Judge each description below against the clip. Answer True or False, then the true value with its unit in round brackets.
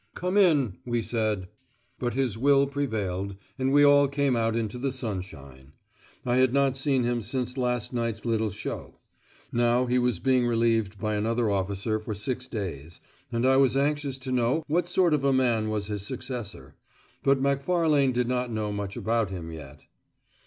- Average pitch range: True (3.9 semitones)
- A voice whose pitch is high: False (120 Hz)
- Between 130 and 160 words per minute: False (175 wpm)